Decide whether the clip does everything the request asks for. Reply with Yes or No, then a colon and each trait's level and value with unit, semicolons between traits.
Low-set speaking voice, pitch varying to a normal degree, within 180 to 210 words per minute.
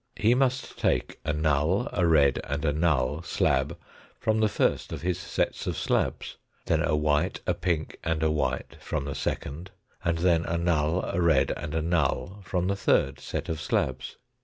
Yes: very low, 80 Hz; average, 3.1 semitones; average, 185 wpm